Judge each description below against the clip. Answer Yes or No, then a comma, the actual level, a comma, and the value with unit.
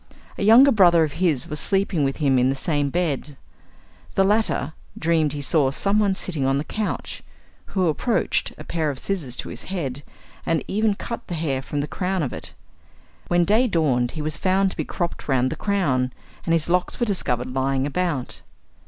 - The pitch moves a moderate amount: No, wide, 5.8 semitones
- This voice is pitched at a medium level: Yes, medium, 160 Hz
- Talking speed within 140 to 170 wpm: No, average, 195 wpm